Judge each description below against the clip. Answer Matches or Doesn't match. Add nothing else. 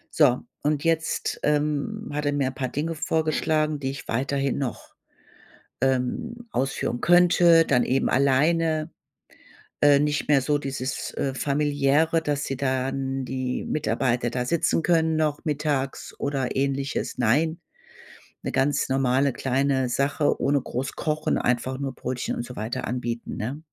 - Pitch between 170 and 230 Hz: Doesn't match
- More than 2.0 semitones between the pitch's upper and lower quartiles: Matches